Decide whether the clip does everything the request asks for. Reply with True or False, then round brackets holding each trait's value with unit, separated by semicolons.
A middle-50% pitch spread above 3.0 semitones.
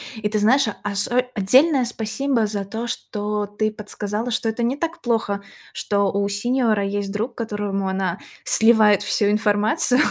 False (2.6 semitones)